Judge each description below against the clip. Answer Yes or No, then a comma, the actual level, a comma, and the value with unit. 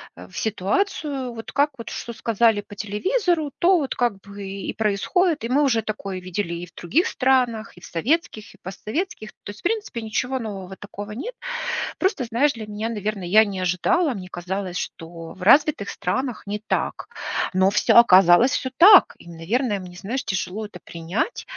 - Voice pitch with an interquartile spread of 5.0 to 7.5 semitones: Yes, wide, 5.5 semitones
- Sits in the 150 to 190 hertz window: No, high, 215 Hz